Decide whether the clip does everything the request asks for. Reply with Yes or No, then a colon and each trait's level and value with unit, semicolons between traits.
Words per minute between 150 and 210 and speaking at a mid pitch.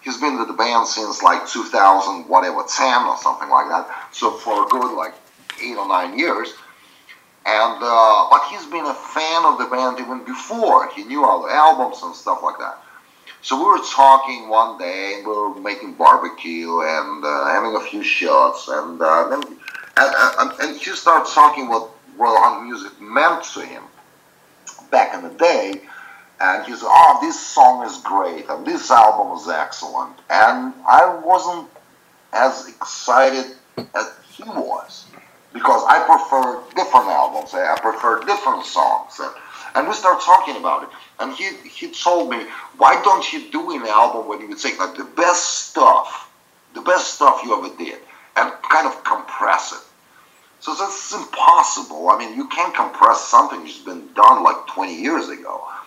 Yes: average, 175 wpm; medium, 175 Hz